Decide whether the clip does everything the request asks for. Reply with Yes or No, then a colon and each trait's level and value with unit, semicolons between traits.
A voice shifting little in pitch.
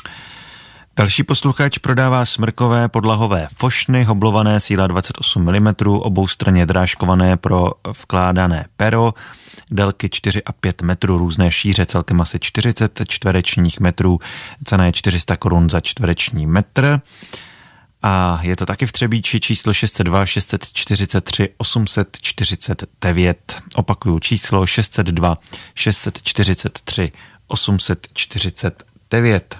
No: average, 3.8 semitones